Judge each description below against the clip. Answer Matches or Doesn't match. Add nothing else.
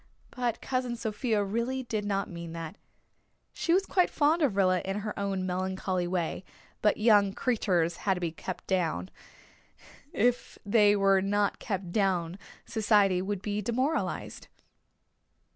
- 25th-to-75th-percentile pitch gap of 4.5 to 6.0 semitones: Doesn't match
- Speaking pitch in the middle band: Doesn't match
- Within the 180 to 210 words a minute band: Doesn't match